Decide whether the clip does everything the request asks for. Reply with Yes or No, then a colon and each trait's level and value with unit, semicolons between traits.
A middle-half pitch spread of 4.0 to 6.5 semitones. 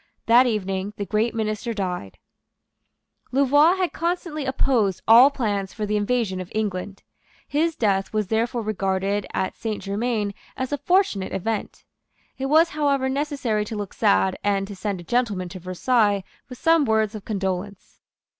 Yes: average, 4.9 semitones